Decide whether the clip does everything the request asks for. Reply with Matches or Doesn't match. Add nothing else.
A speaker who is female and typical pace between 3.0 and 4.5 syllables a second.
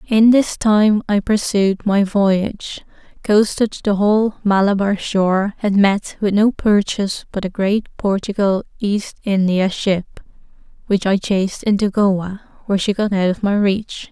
Matches